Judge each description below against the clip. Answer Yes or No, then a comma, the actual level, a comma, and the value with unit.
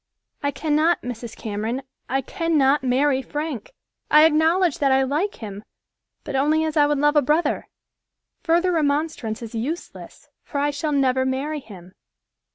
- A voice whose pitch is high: Yes, very high, 285 Hz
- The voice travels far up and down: No, average, 3.2 semitones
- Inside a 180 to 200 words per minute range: No, average, 155 wpm